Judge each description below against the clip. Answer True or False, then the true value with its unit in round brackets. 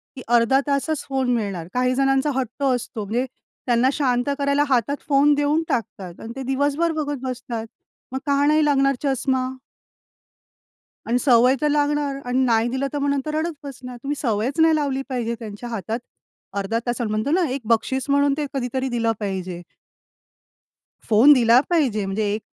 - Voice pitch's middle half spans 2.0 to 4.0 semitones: True (3.4 semitones)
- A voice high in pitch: True (260 Hz)